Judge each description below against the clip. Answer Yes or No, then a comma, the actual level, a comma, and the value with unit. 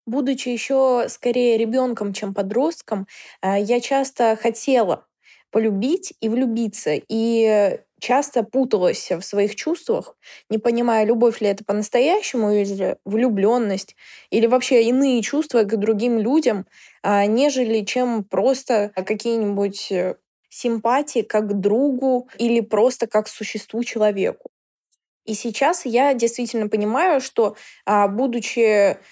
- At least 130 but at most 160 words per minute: No, slow, 110 wpm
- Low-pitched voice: No, high, 230 Hz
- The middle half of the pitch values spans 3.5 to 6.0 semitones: No, average, 3.0 semitones